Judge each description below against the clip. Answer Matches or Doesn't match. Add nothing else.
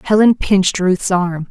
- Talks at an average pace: Matches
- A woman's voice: Matches